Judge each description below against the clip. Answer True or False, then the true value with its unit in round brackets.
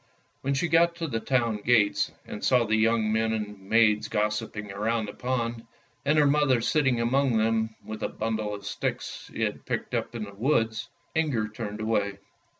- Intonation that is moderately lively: True (3.1 semitones)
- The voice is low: True (115 Hz)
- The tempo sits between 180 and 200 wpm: True (185 wpm)